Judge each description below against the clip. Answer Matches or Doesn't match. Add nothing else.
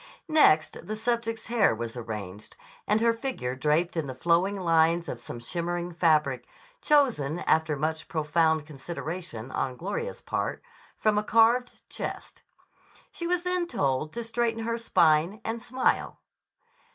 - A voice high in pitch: Doesn't match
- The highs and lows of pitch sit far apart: Matches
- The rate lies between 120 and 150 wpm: Matches